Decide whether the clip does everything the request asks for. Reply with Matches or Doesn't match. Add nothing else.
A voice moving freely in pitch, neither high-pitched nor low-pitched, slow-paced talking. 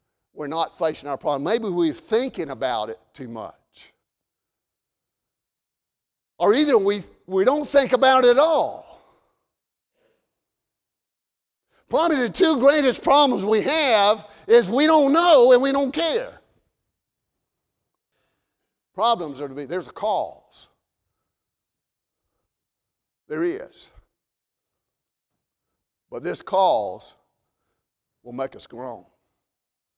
Doesn't match